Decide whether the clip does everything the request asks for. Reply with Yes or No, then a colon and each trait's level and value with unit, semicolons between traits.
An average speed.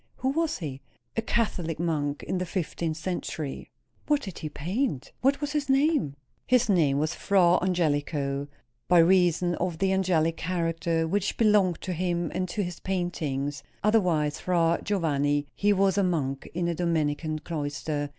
Yes: average, 160 wpm